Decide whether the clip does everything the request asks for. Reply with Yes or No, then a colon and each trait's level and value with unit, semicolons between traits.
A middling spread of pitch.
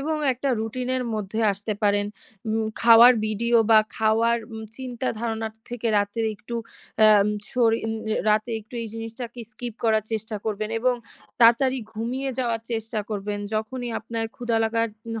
No: narrow, 1.9 semitones